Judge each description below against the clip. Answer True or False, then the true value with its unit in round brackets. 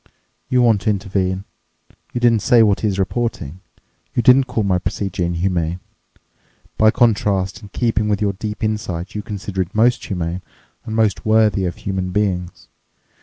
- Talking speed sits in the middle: True (155 wpm)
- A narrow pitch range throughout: False (3.0 semitones)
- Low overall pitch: True (100 Hz)